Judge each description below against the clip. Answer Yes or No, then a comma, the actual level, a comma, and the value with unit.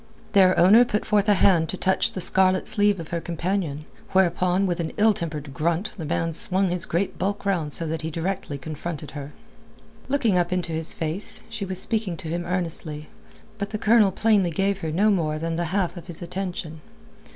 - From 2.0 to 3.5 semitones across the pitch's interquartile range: Yes, average, 3.2 semitones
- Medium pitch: Yes, medium, 180 Hz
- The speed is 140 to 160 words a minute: No, average, 200 wpm